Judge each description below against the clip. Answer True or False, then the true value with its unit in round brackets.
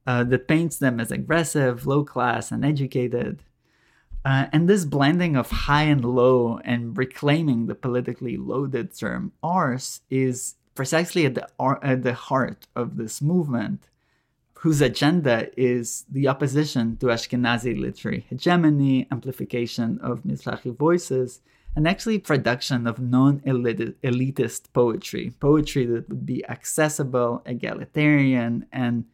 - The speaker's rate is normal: False (125 wpm)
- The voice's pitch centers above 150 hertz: False (130 Hz)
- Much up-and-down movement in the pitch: False (3.2 semitones)